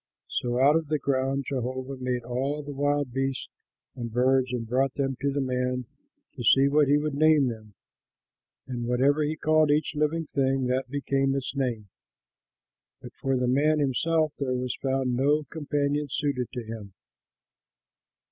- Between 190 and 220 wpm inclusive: No, average, 165 wpm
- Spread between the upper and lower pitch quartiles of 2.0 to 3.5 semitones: Yes, narrow, 2.4 semitones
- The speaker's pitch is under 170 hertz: Yes, low, 135 Hz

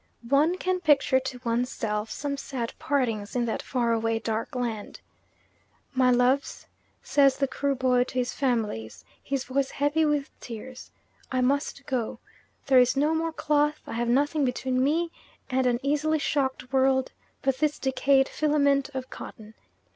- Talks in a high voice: Yes, very high, 265 Hz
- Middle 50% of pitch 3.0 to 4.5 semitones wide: No, narrow, 2.4 semitones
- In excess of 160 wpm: No, average, 155 wpm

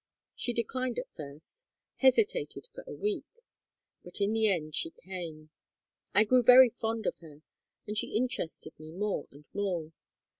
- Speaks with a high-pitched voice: Yes, high, 210 Hz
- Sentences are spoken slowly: No, average, 155 wpm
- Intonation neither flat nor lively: No, wide, 7.6 semitones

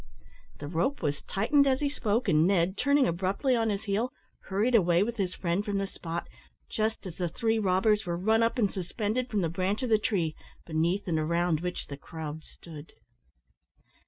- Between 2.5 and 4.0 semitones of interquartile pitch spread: No, average, 4.6 semitones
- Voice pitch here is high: Yes, high, 195 Hz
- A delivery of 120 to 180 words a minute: No, average, 190 wpm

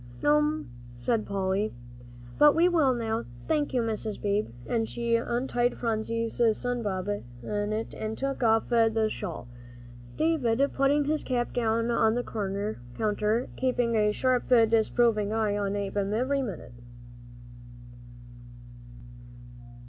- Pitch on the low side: No, high, 225 Hz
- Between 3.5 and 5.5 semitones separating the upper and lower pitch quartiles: No, average, 2.8 semitones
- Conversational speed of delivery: No, slow, 120 wpm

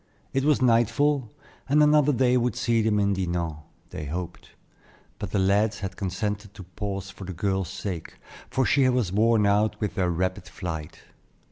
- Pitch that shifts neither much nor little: Yes, average, 4.3 semitones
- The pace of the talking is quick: No, average, 170 wpm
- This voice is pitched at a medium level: No, low, 100 Hz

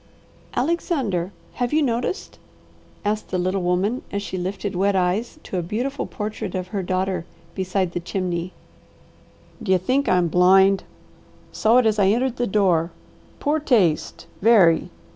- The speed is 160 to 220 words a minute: No, average, 145 wpm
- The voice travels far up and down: No, average, 4.2 semitones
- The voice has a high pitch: Yes, high, 195 Hz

